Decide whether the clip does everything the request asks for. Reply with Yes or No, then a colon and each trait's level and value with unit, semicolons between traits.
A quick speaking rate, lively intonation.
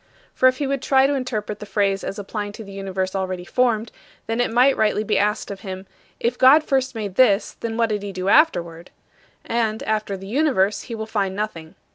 No: fast, 215 wpm; average, 3.9 semitones